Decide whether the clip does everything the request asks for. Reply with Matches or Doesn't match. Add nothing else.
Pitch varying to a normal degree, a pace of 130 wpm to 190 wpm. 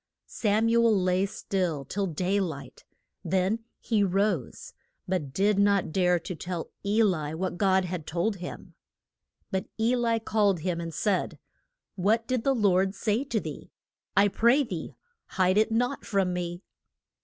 Matches